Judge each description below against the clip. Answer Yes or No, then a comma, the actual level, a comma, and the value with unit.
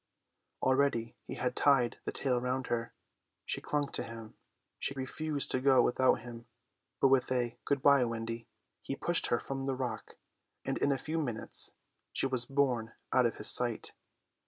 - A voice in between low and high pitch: No, low, 130 Hz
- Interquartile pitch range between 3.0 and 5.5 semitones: No, narrow, 2.4 semitones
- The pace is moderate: Yes, average, 175 wpm